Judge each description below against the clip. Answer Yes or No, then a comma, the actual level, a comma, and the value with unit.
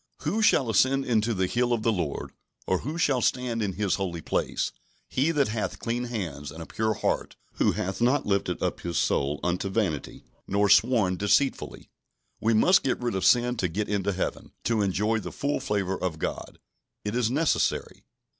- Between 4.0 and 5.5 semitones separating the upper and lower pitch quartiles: Yes, average, 4.5 semitones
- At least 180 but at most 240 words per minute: Yes, average, 190 wpm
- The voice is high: No, low, 110 Hz